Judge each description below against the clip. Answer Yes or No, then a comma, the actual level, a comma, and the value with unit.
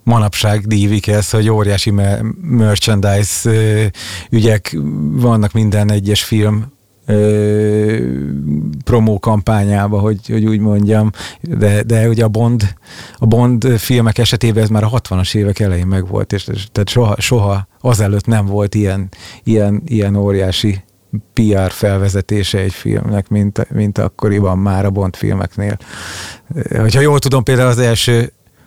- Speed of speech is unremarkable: Yes, average, 125 wpm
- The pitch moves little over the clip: Yes, narrow, 1.9 semitones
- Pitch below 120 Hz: Yes, low, 105 Hz